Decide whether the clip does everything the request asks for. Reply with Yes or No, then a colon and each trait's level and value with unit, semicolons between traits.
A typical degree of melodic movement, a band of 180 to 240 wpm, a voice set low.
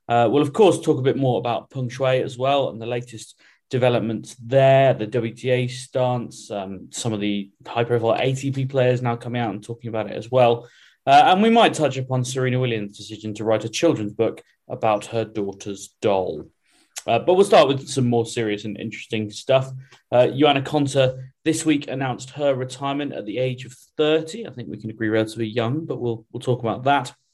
Yes: average, 3.1 semitones; average, 200 wpm; low, 125 Hz